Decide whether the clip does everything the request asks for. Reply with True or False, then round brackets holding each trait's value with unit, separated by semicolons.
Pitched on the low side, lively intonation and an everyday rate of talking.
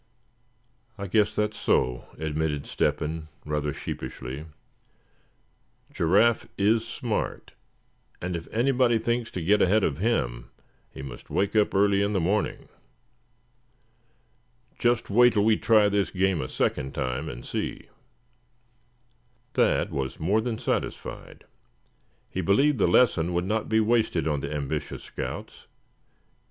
False (100 Hz; 6.1 semitones; 130 wpm)